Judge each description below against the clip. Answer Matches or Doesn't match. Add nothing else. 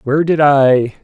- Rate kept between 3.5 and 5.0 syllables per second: Matches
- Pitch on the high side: Doesn't match